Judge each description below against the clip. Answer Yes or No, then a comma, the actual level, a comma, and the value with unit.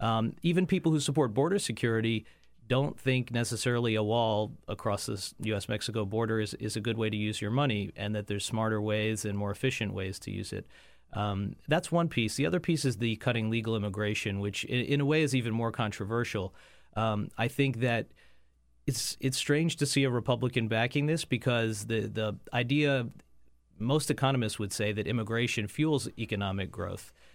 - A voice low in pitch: Yes, low, 115 Hz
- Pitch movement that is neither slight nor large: Yes, average, 3.8 semitones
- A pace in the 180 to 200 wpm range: Yes, average, 185 wpm